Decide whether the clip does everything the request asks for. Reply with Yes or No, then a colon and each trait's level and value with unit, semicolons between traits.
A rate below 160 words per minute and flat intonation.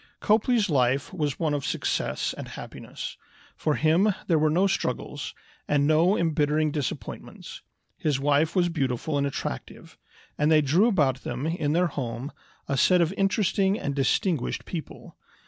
No: average, 150 wpm; average, 4.2 semitones